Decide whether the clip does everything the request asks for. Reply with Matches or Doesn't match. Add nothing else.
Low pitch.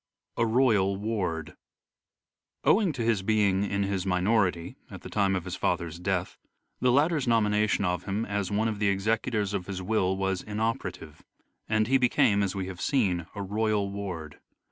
Matches